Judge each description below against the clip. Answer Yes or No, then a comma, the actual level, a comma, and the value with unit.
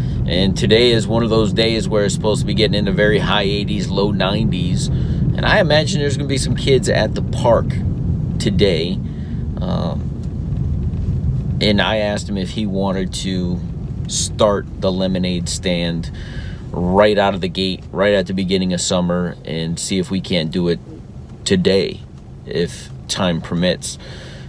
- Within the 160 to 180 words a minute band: Yes, average, 165 wpm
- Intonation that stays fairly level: Yes, narrow, 2.3 semitones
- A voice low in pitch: Yes, very low, 95 Hz